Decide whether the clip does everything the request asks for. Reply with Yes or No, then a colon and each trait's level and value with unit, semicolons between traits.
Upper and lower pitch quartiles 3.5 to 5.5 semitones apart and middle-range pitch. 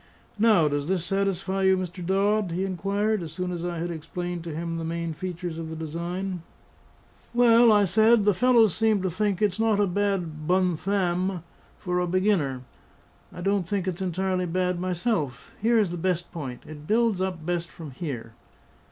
No: average, 3.0 semitones; medium, 180 Hz